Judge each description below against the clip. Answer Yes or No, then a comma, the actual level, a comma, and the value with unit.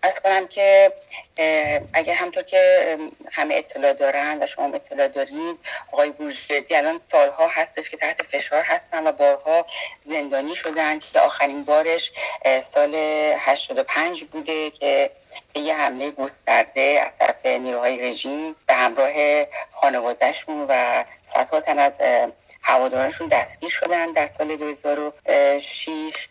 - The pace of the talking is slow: Yes, slow, 120 wpm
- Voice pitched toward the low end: No, medium, 155 Hz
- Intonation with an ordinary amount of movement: Yes, average, 3.5 semitones